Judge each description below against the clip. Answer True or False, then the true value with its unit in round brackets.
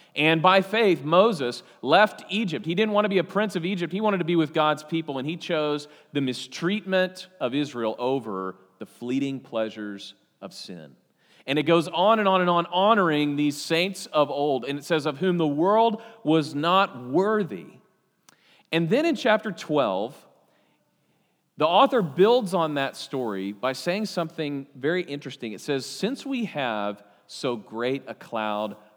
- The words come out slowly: False (170 wpm)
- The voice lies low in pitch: False (160 Hz)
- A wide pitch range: True (6.0 semitones)